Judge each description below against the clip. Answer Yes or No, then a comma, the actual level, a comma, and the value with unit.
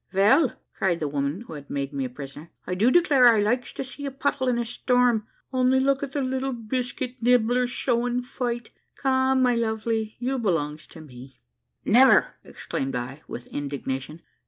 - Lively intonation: Yes, wide, 8.7 semitones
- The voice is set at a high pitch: Yes, high, 235 Hz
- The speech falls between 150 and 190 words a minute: Yes, average, 180 wpm